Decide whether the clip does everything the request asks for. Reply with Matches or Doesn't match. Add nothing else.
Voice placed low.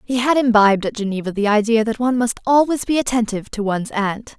Doesn't match